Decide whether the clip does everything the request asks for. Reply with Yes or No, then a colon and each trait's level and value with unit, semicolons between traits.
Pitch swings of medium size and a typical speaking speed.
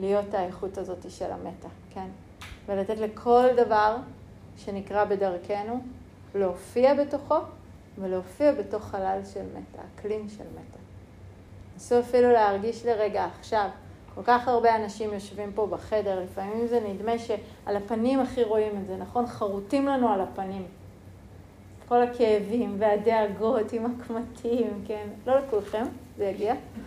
Yes: average, 3.6 semitones; average, 125 wpm